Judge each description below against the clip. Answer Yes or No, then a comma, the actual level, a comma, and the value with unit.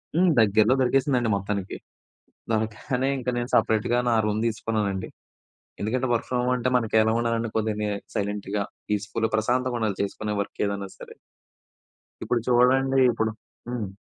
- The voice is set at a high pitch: No, low, 110 Hz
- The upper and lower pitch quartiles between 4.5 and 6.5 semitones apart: No, average, 2.9 semitones